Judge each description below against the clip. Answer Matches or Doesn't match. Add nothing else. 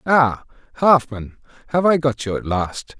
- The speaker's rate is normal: Matches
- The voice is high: Doesn't match